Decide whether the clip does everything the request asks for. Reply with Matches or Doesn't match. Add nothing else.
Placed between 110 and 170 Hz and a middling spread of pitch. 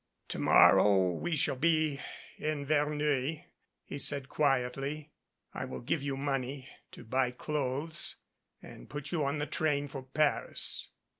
Doesn't match